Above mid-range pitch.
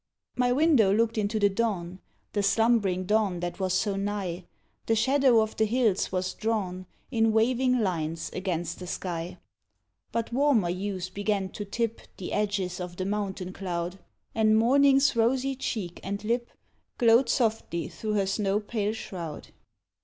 Yes: high, 205 Hz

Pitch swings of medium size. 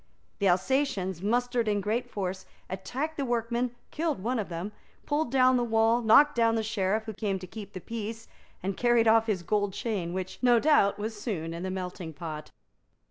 Yes: average, 4.2 semitones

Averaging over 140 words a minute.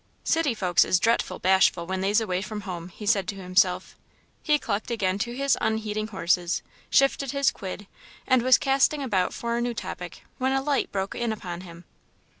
Yes: average, 190 wpm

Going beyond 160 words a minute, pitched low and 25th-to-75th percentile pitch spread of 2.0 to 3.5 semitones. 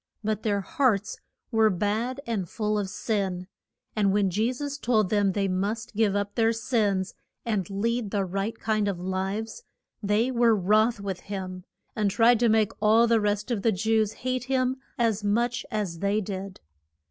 No: average, 175 wpm; high, 215 Hz; narrow, 2.5 semitones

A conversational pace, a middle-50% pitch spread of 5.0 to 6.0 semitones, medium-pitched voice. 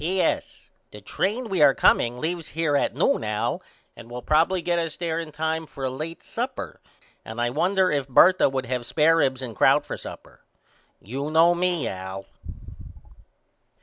Yes: average, 180 wpm; average, 5.3 semitones; medium, 155 Hz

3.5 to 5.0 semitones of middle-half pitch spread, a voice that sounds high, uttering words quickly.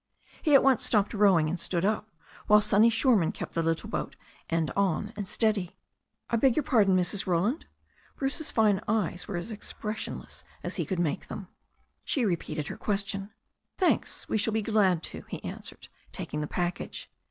No: average, 3.8 semitones; high, 205 Hz; average, 175 wpm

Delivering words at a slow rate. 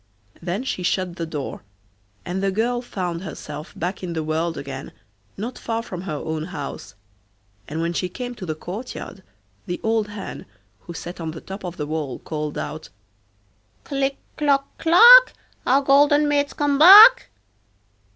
No: average, 160 wpm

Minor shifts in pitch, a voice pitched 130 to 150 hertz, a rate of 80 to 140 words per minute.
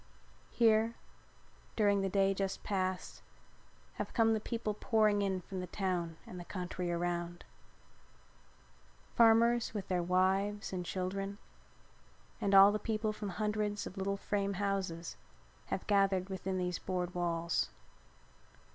No: narrow, 2.3 semitones; high, 195 Hz; slow, 135 wpm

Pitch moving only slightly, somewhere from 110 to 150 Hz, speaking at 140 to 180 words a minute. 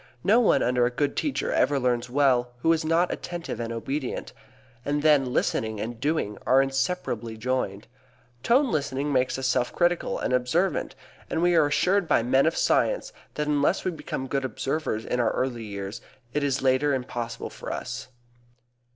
No: average, 4.3 semitones; low, 135 Hz; average, 175 wpm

